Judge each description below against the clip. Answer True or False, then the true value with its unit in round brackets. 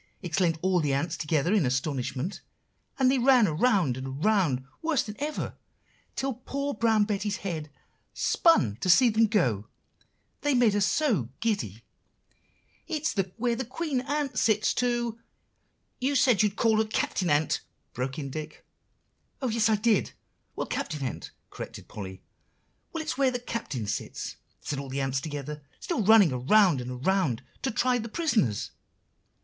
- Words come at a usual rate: True (160 wpm)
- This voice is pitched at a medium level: False (205 Hz)